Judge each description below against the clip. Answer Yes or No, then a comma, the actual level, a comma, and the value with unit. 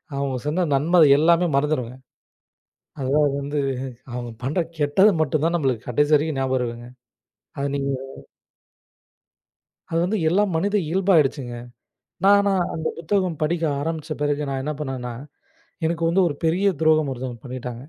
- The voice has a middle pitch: Yes, medium, 150 Hz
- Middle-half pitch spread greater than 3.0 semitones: Yes, average, 4.0 semitones